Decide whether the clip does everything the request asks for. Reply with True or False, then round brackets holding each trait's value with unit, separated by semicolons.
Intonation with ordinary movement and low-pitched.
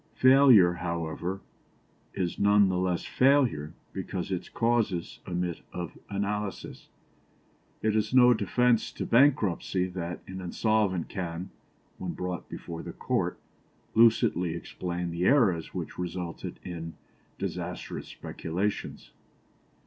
True (3.9 semitones; 95 Hz)